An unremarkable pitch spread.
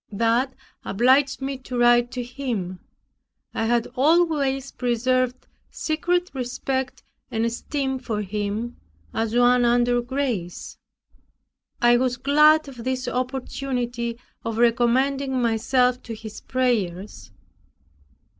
No: narrow, 2.3 semitones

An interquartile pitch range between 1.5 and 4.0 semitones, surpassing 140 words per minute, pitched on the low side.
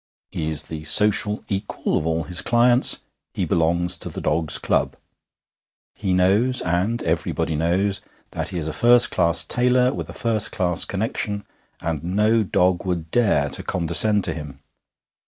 No: average, 4.6 semitones; average, 160 wpm; very low, 90 Hz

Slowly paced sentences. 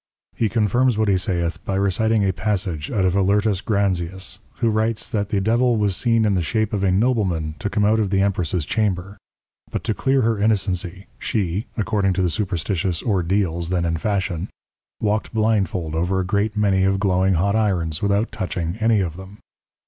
No: average, 190 wpm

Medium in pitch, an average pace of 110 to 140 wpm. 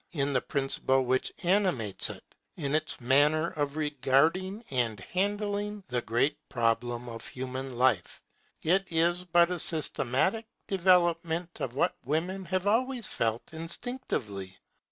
Yes: medium, 155 Hz; slow, 135 wpm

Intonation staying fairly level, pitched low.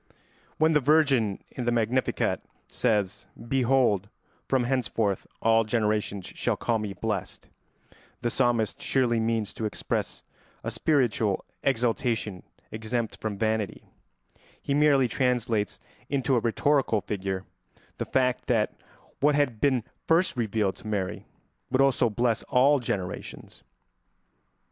No: average, 3.6 semitones; low, 115 Hz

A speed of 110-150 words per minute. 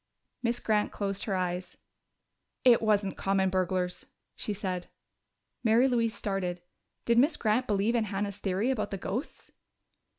Yes: average, 140 wpm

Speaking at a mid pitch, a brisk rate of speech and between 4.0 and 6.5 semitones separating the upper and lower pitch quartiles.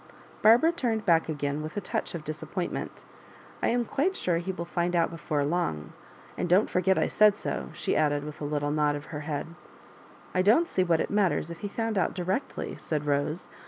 Yes: medium, 170 Hz; fast, 215 wpm; average, 4.8 semitones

